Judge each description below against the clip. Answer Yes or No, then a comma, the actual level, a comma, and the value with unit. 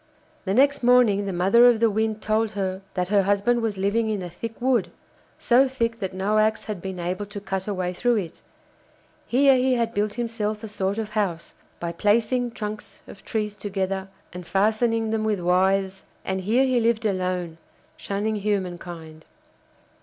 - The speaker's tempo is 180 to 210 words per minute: Yes, average, 185 wpm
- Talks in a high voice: Yes, high, 210 Hz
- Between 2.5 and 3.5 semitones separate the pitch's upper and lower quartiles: Yes, average, 3.2 semitones